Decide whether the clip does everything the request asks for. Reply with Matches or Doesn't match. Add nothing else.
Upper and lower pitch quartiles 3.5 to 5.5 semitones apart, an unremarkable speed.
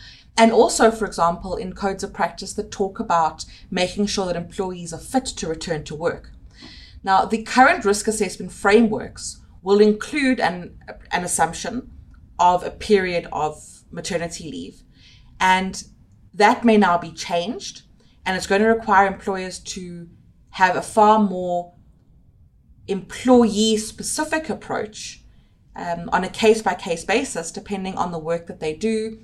Matches